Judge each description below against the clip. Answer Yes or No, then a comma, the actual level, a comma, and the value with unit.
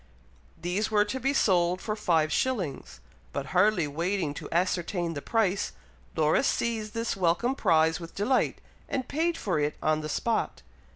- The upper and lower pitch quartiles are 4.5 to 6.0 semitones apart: Yes, average, 5.3 semitones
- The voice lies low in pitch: No, medium, 185 Hz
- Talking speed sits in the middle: Yes, average, 160 wpm